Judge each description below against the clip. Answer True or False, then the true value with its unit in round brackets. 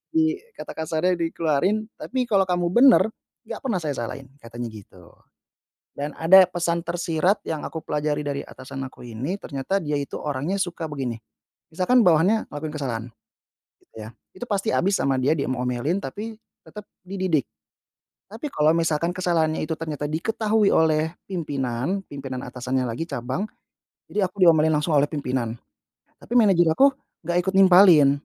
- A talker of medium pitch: True (160 Hz)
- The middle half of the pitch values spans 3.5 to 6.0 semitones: True (5.2 semitones)